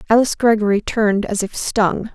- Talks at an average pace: Yes, average, 170 wpm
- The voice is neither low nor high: No, high, 215 Hz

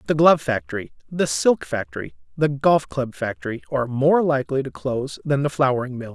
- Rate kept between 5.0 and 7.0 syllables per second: Yes, 5.7 syllables/s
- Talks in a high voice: No, low, 130 Hz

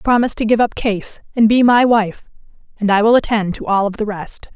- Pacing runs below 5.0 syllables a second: No, 5.5 syllables/s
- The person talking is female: Yes, female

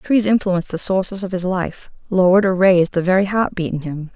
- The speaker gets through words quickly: Yes, fast, 230 wpm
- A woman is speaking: Yes, female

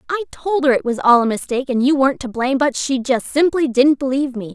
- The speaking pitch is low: No, very high, 270 Hz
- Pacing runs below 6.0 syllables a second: No, 6.4 syllables/s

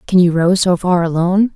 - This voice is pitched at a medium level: Yes, medium, 180 Hz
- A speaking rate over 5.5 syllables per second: Yes, 5.7 syllables/s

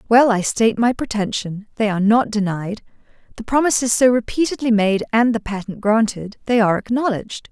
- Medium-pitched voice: No, high, 220 Hz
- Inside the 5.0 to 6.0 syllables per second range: Yes, 5.7 syllables/s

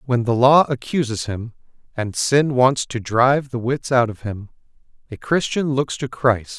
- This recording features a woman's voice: No, male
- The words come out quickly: No, average, 180 wpm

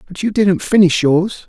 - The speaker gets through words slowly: No, fast, 205 wpm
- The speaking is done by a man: Yes, male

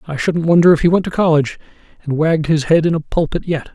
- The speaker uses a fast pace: Yes, fast, 255 wpm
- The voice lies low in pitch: No, medium, 160 Hz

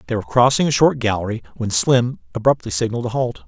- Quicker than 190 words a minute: Yes, fast, 205 wpm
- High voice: No, low, 120 Hz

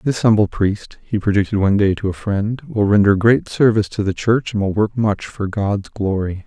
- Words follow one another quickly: Yes, fast, 225 wpm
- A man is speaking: Yes, male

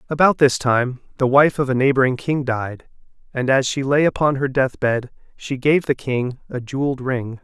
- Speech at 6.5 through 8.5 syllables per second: No, 4.9 syllables/s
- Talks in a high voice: No, low, 135 Hz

